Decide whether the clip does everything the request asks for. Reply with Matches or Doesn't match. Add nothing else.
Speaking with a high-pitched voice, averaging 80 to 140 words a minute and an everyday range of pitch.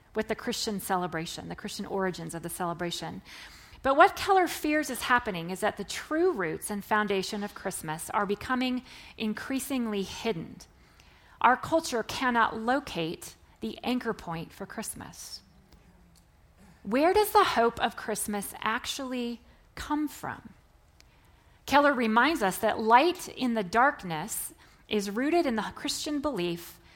Doesn't match